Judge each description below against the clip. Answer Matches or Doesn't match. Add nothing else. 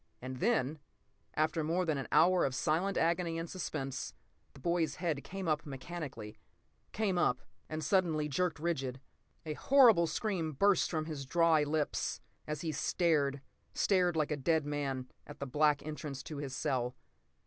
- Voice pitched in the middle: Matches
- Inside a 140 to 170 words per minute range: Matches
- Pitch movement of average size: Matches